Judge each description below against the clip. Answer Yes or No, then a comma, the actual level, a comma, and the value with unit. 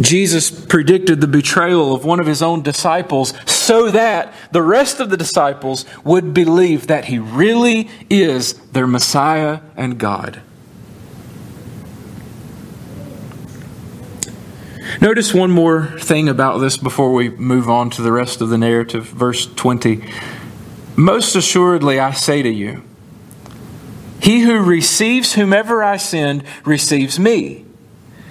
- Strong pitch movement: Yes, wide, 6.2 semitones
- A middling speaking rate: No, slow, 125 wpm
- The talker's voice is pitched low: No, medium, 150 Hz